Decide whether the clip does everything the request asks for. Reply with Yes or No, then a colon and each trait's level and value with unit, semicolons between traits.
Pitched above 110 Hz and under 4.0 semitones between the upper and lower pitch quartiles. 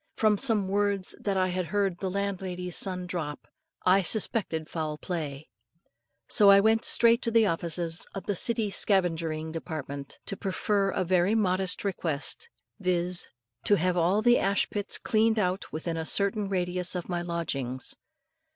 Yes: medium, 185 Hz; average, 3.0 semitones